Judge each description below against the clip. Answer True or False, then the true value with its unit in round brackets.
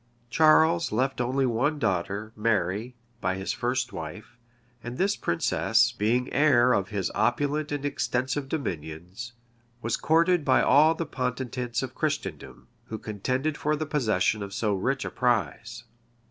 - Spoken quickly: False (145 wpm)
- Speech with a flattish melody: False (5.1 semitones)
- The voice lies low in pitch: True (125 Hz)